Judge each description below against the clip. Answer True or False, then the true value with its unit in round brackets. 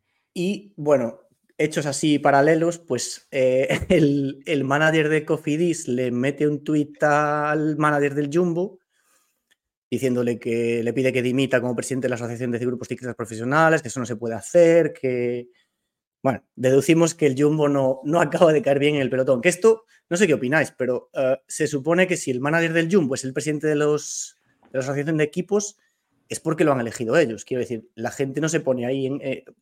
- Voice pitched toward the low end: False (145 Hz)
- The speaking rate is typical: False (200 wpm)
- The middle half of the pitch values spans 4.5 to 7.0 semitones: False (3.9 semitones)